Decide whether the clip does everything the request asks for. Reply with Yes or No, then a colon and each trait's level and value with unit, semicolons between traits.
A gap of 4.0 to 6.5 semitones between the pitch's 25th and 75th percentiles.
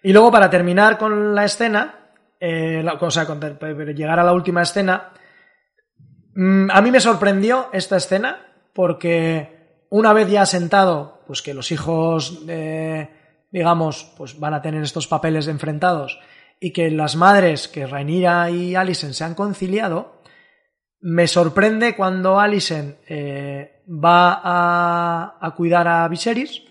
No: average, 3.6 semitones